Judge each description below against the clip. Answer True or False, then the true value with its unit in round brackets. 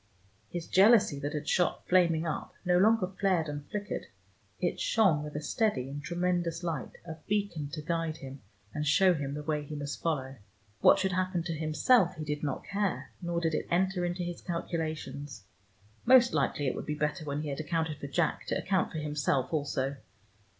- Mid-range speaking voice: True (160 Hz)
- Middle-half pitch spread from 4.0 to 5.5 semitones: False (3.5 semitones)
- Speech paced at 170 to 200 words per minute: True (190 wpm)